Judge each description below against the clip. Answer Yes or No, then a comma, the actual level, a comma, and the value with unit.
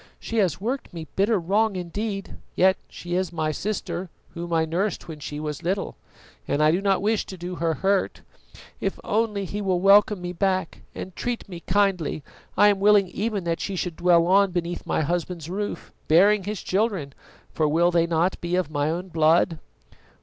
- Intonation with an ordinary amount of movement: Yes, average, 3.1 semitones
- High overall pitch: No, medium, 180 Hz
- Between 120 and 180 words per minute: No, average, 190 wpm